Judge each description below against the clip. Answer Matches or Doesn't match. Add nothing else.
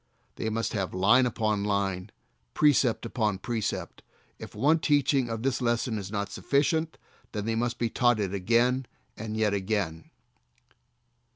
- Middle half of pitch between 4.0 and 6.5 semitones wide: Doesn't match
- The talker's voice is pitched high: Doesn't match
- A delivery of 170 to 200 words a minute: Doesn't match